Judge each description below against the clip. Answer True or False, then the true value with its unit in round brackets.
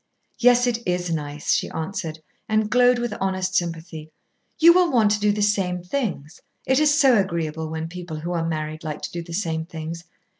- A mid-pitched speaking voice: True (180 Hz)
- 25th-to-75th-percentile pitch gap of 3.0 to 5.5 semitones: True (5.2 semitones)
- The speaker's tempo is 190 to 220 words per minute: True (195 wpm)